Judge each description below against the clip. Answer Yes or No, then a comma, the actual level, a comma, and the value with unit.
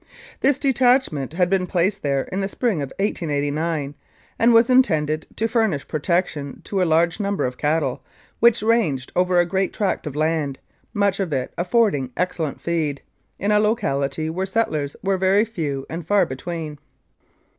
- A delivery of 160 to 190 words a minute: Yes, average, 165 wpm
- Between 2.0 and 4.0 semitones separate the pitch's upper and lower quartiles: No, wide, 5.4 semitones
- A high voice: No, medium, 175 Hz